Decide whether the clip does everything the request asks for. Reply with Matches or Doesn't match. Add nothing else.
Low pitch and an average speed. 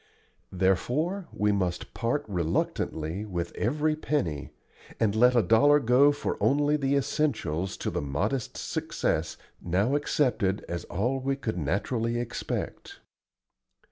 Doesn't match